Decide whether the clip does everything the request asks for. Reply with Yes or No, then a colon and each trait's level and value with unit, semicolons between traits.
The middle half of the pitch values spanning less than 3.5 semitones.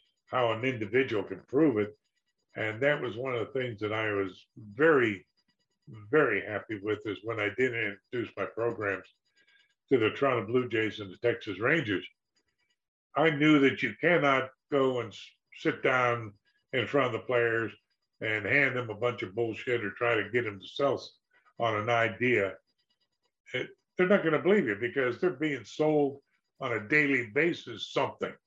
No: average, 4.2 semitones